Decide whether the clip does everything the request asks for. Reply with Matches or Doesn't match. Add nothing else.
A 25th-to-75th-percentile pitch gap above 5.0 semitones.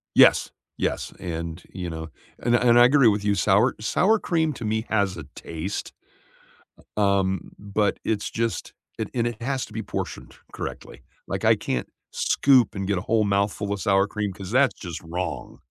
Doesn't match